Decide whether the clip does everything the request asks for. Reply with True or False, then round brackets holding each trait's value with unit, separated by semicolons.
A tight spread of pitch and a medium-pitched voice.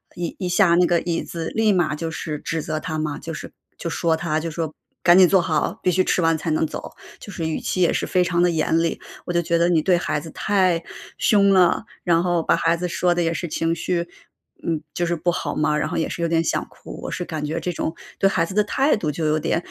True (1.7 semitones; 170 Hz)